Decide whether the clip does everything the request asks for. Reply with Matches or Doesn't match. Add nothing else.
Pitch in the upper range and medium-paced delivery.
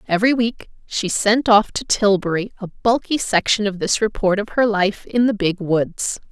Matches